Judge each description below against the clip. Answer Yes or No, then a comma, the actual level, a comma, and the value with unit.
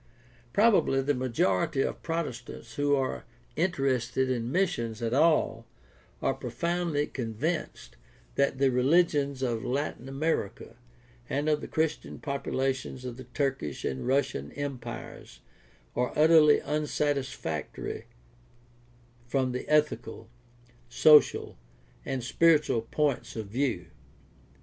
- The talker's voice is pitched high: No, low, 135 Hz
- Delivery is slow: Yes, slow, 105 wpm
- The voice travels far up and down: No, average, 3.8 semitones